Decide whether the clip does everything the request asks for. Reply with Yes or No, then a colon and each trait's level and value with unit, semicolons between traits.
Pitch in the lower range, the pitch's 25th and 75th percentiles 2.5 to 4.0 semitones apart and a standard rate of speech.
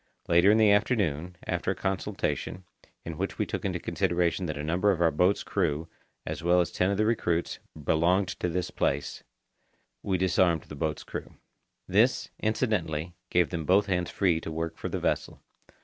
Yes: very low, 90 Hz; average, 2.8 semitones; average, 180 wpm